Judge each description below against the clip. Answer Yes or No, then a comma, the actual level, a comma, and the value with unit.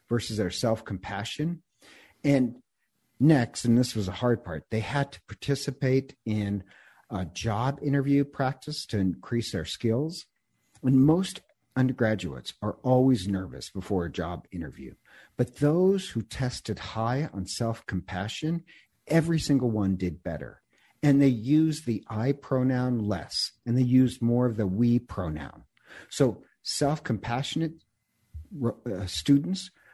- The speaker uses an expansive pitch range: Yes, wide, 5.7 semitones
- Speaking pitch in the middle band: No, low, 120 Hz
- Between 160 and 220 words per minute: No, slow, 135 wpm